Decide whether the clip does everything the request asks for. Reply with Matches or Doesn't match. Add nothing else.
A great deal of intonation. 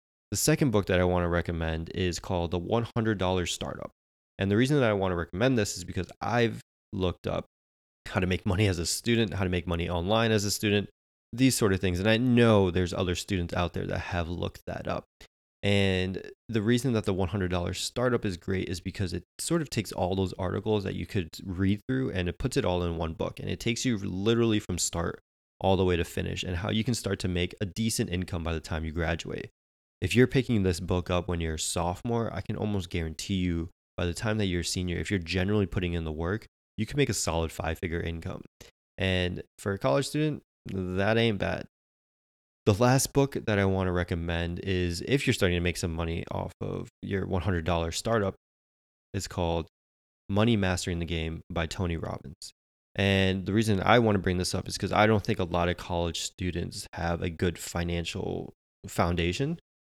Doesn't match